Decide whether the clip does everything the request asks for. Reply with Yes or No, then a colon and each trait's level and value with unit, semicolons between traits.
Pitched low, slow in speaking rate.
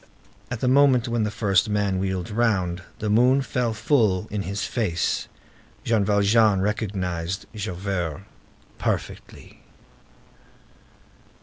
Yes: low, 105 Hz; slow, 110 wpm